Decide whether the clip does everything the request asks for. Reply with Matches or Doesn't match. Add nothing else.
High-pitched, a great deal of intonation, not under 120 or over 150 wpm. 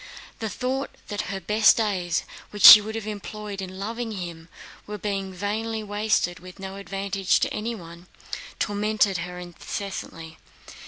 Doesn't match